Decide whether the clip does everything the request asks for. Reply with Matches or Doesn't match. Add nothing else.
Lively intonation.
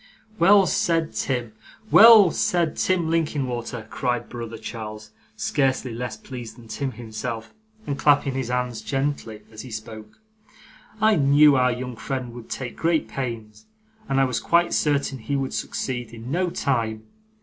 Doesn't match